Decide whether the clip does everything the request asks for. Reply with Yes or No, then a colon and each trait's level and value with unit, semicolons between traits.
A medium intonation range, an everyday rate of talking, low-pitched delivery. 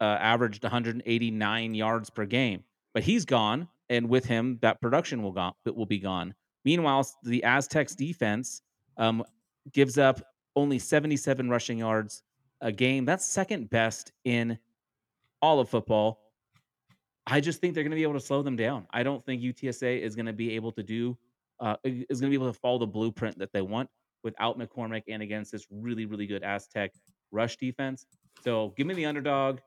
Yes: average, 3.3 semitones; average, 185 wpm; low, 120 Hz